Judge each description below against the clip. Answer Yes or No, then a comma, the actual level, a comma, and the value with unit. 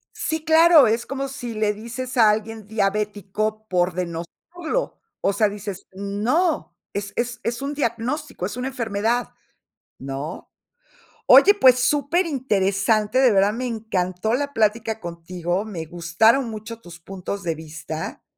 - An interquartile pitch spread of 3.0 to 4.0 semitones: No, average, 4.6 semitones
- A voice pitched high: Yes, high, 215 Hz